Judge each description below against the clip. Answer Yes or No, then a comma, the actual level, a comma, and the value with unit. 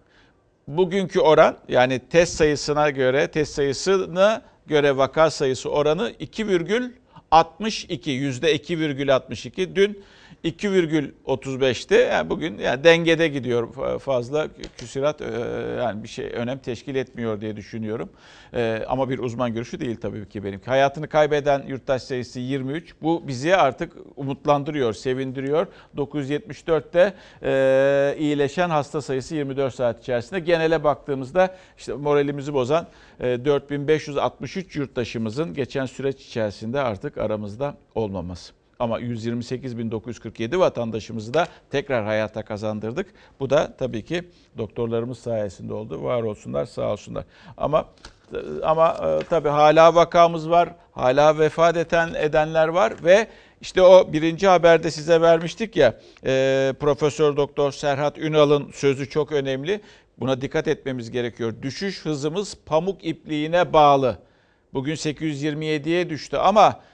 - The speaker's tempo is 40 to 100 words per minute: No, average, 115 wpm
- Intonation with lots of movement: No, average, 4.5 semitones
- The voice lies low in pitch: No, medium, 145 Hz